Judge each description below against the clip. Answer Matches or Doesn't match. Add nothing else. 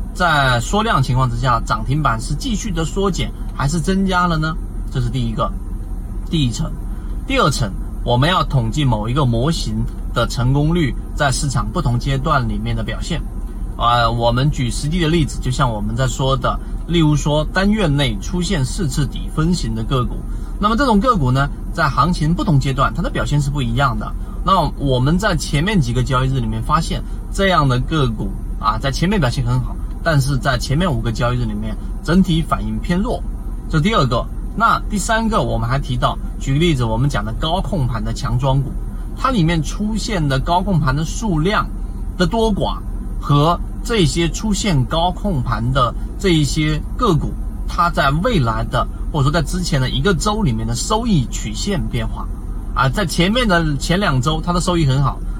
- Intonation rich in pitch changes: Matches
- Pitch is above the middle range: Doesn't match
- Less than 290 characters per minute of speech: Matches